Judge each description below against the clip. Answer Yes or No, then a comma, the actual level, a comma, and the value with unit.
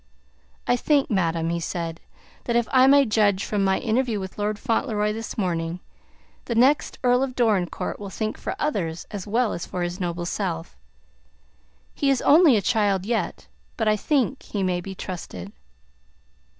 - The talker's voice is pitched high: Yes, high, 210 Hz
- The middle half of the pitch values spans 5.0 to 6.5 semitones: Yes, average, 5.3 semitones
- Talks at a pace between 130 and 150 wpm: No, average, 170 wpm